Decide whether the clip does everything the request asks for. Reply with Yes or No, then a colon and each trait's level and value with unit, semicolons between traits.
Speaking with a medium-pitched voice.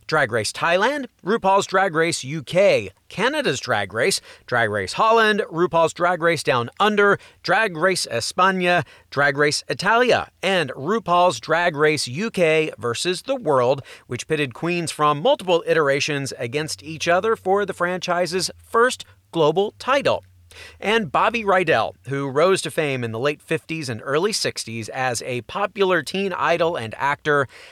Yes: medium, 165 Hz